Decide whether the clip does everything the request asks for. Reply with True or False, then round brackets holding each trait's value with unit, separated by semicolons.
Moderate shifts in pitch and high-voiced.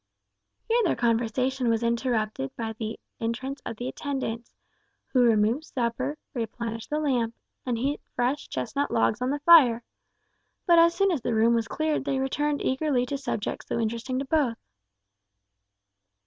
True (3.7 semitones; 250 Hz)